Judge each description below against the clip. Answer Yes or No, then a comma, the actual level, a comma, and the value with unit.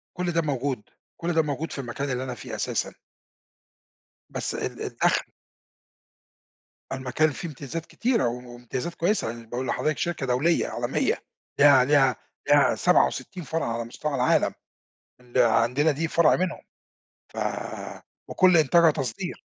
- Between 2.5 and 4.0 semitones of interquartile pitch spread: No, average, 4.7 semitones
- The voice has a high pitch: No, medium, 145 Hz